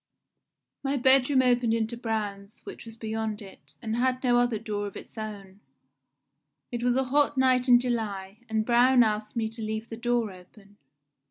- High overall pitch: Yes, high, 225 Hz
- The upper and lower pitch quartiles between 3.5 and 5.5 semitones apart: No, narrow, 2.5 semitones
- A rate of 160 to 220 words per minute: Yes, average, 175 wpm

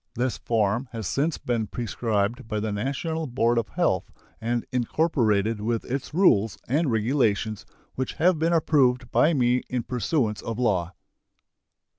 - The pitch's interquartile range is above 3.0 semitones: Yes, average, 3.9 semitones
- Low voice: Yes, low, 120 Hz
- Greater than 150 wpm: No, average, 145 wpm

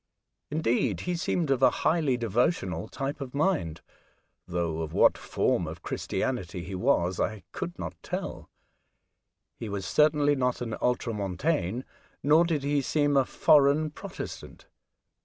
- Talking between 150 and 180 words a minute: No, average, 140 wpm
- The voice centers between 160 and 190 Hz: No, low, 130 Hz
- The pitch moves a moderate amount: No, wide, 7.0 semitones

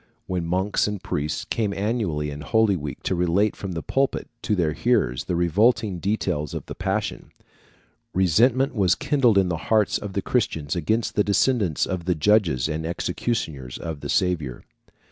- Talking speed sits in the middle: Yes, average, 170 wpm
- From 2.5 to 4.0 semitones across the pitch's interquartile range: No, average, 4.9 semitones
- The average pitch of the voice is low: Yes, very low, 95 Hz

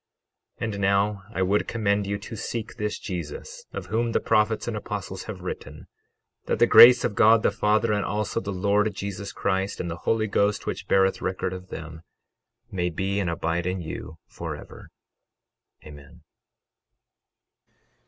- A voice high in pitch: No, low, 100 Hz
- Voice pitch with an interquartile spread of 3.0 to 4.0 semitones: No, narrow, 2.4 semitones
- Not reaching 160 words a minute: No, average, 165 wpm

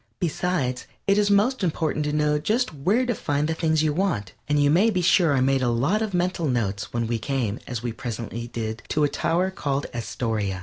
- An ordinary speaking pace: No, fast, 220 wpm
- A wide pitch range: Yes, wide, 7.1 semitones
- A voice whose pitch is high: No, medium, 150 Hz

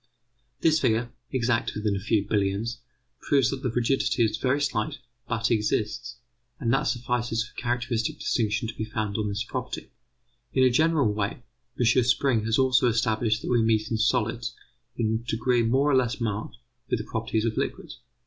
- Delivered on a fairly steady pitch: Yes, narrow, 2.3 semitones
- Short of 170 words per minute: No, average, 180 wpm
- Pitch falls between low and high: No, low, 115 Hz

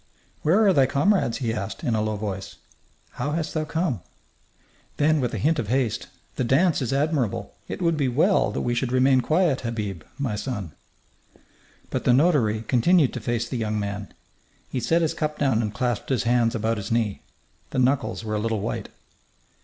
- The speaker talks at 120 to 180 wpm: No, average, 190 wpm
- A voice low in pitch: Yes, low, 125 Hz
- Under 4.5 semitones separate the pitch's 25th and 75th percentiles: No, average, 5.3 semitones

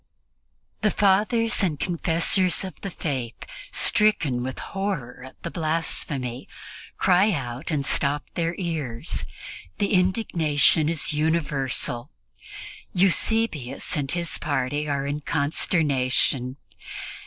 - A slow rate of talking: Yes, slow, 105 wpm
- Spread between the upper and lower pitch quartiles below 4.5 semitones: No, average, 5.0 semitones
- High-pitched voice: No, medium, 155 Hz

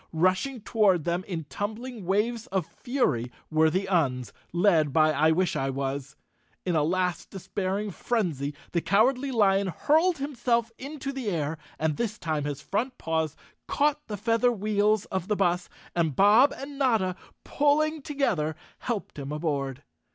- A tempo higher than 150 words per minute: Yes, average, 160 wpm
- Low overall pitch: No, high, 195 Hz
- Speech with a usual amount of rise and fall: No, wide, 7.0 semitones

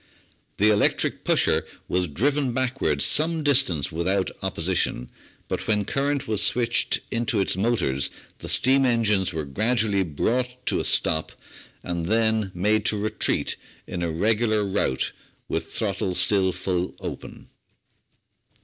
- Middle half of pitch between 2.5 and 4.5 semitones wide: No, average, 4.9 semitones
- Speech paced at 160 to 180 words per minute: No, slow, 135 wpm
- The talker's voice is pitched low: Yes, low, 105 Hz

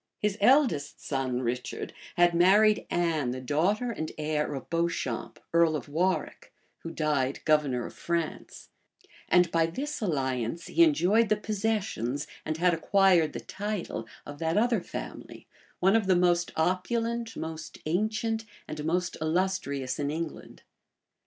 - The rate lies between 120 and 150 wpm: Yes, average, 140 wpm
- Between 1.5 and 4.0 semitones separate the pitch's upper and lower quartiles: No, wide, 5.4 semitones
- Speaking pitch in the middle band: Yes, medium, 170 Hz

